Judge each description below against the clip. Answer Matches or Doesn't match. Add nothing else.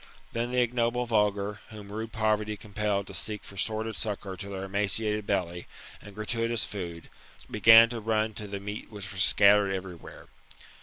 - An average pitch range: Doesn't match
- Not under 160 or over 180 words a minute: Matches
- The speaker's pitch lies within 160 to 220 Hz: Doesn't match